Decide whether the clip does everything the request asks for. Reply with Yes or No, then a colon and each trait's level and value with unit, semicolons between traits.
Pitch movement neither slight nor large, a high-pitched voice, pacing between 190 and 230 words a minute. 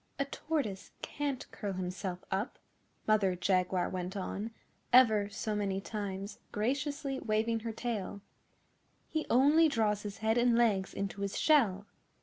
No: average, 3.9 semitones; high, 215 Hz; slow, 135 wpm